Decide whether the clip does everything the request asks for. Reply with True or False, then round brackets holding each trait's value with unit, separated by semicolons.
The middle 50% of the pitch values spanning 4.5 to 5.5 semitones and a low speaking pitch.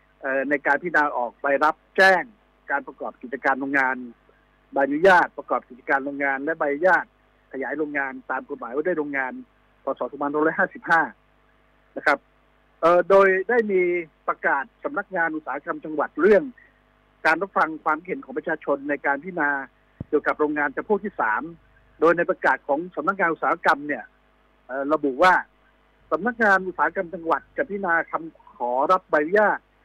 False (4.8 semitones; 155 Hz)